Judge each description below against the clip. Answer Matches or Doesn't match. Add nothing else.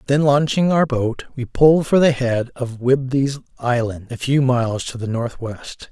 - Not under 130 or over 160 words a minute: Doesn't match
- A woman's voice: Doesn't match